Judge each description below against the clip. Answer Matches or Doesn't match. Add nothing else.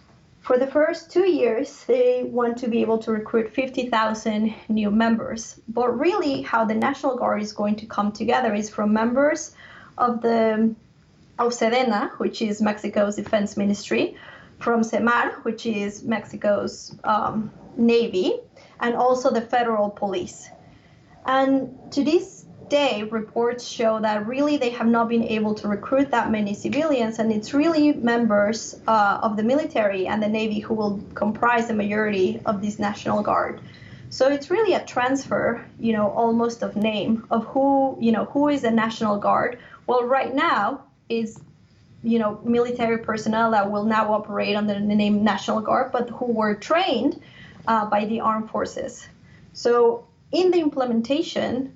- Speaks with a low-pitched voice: Doesn't match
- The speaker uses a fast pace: Doesn't match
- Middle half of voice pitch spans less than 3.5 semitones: Matches